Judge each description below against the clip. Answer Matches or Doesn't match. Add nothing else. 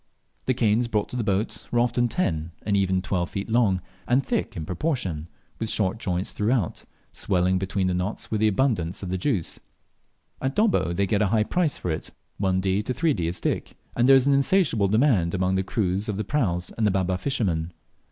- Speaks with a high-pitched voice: Doesn't match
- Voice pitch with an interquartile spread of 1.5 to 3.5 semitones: Doesn't match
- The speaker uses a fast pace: Matches